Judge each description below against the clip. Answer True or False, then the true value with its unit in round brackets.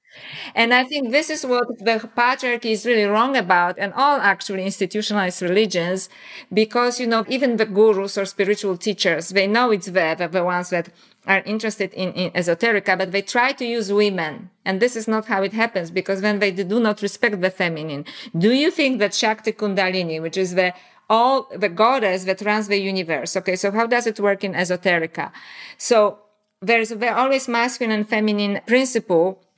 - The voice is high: True (205 Hz)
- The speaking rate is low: False (185 wpm)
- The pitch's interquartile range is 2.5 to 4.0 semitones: True (3.5 semitones)